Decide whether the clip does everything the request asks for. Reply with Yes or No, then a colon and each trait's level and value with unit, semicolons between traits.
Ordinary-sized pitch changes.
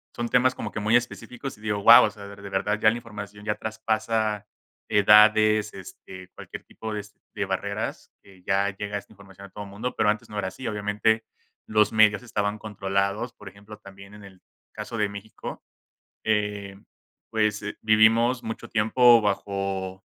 No: narrow, 1.6 semitones